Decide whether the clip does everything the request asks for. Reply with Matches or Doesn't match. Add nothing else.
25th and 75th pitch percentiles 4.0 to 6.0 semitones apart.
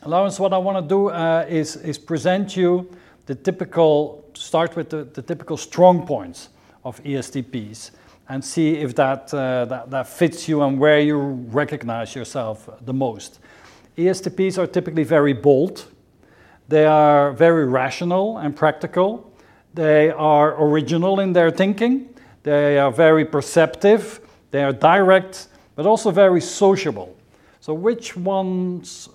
Matches